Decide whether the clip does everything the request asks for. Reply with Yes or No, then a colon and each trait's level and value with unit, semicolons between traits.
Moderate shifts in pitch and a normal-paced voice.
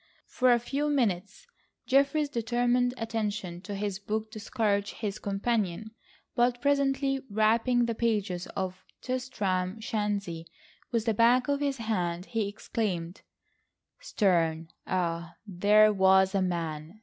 No: average, 4.3 semitones; slow, 125 wpm